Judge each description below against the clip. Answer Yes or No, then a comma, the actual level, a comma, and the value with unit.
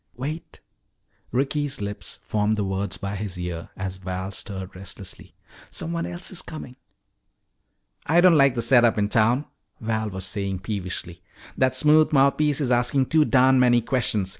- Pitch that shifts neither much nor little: No, wide, 6.1 semitones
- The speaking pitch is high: No, low, 115 Hz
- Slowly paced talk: No, average, 160 wpm